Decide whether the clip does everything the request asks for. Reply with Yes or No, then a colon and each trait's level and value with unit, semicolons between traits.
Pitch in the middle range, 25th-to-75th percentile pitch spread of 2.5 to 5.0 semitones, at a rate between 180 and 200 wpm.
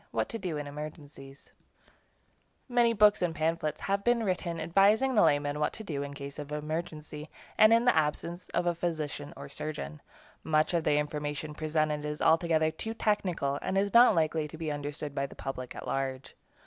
Yes: medium, 155 Hz; average, 3.6 semitones; average, 190 wpm